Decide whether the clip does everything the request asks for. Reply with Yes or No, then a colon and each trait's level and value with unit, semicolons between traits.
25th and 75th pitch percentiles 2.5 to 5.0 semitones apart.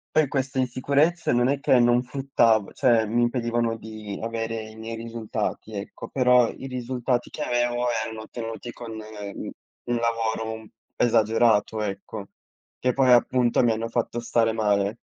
No: narrow, 1.9 semitones